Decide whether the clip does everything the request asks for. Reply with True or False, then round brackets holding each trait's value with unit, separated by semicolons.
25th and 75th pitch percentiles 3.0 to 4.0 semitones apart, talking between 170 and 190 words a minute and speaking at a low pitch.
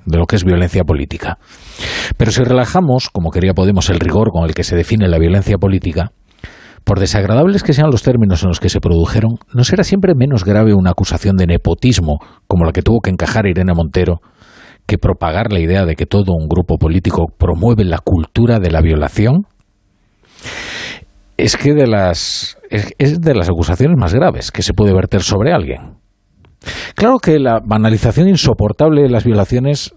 False (4.8 semitones; 180 wpm; 100 Hz)